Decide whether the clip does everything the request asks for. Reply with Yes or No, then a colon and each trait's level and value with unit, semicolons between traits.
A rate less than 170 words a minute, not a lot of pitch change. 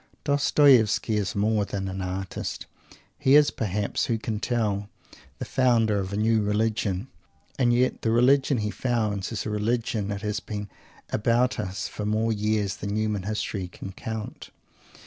Yes: average, 160 wpm; narrow, 2.2 semitones